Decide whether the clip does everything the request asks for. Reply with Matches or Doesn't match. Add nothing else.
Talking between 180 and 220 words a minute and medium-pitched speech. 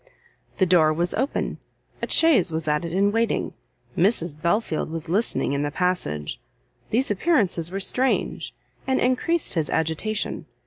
Doesn't match